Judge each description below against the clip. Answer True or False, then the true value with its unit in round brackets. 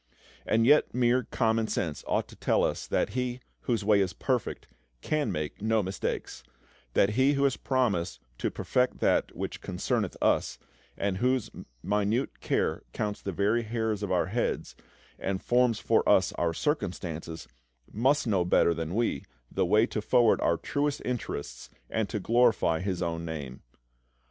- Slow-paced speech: False (160 wpm)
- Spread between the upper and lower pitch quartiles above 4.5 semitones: True (5.3 semitones)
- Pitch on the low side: True (105 Hz)